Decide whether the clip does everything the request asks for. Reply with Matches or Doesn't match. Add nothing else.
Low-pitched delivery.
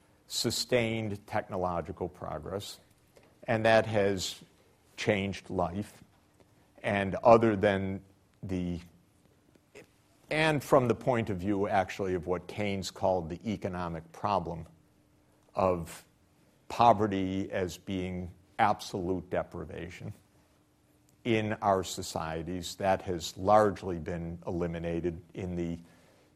Matches